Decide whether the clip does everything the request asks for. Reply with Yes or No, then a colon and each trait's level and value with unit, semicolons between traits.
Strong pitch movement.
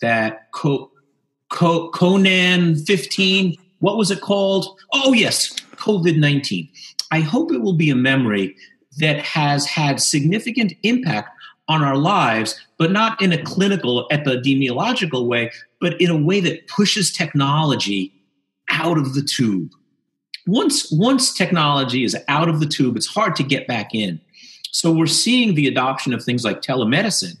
Yes: wide, 6.0 semitones